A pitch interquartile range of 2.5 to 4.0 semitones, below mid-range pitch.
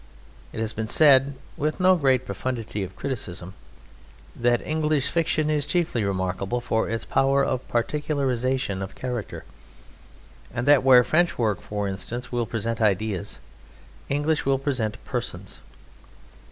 No: average, 4.5 semitones; low, 125 Hz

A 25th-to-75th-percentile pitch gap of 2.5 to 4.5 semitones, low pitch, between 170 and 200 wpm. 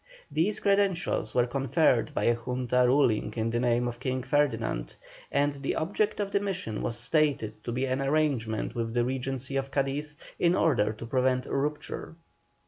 Yes: average, 3.9 semitones; low, 130 Hz; average, 175 wpm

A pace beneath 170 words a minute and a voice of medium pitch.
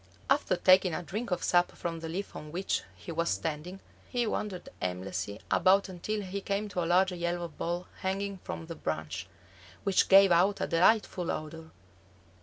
No: average, 175 wpm; medium, 175 Hz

